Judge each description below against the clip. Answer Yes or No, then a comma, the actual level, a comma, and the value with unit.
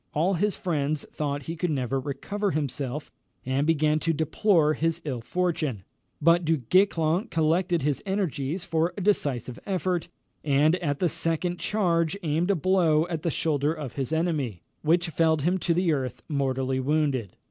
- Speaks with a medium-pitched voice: Yes, medium, 160 Hz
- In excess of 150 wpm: Yes, average, 165 wpm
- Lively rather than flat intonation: No, average, 3.5 semitones